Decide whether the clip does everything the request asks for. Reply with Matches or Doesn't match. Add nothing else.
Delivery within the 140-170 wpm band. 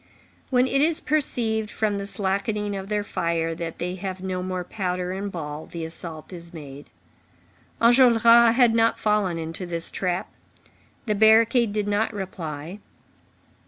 Matches